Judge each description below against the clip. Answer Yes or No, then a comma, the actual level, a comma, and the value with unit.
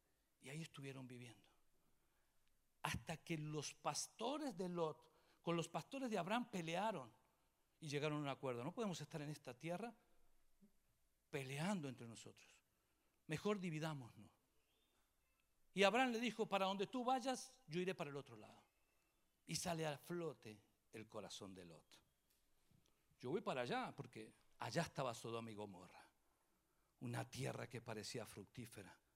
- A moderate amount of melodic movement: No, wide, 7.9 semitones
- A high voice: No, medium, 155 Hz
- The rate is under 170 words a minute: Yes, average, 140 wpm